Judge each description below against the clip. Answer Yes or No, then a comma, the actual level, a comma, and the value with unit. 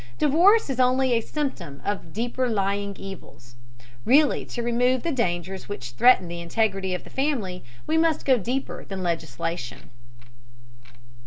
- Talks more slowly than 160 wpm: Yes, average, 145 wpm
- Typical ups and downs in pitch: No, wide, 6.3 semitones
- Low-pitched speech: No, high, 215 Hz